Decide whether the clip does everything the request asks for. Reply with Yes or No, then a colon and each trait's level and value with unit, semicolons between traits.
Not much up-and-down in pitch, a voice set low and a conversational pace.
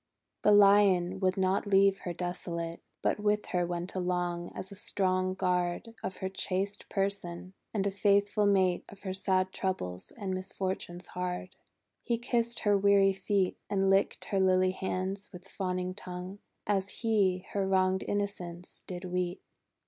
No: narrow, 1.7 semitones; high, 190 Hz; average, 155 wpm